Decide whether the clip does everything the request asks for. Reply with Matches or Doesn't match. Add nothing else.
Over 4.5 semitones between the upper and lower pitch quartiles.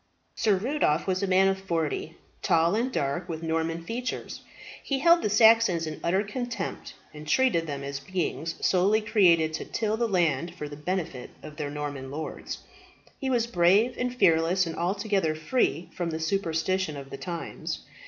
Matches